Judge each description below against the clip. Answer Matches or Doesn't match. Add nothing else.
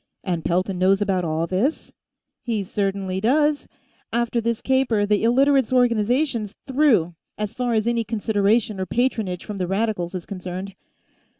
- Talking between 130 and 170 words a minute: Matches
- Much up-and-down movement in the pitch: Doesn't match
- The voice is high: Matches